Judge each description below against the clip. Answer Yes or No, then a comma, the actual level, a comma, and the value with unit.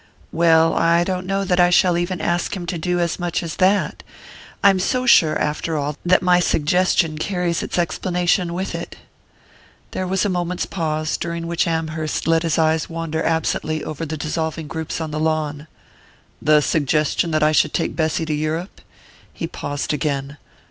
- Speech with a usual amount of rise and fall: No, narrow, 2.3 semitones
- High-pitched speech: No, medium, 165 Hz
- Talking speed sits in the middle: Yes, average, 175 wpm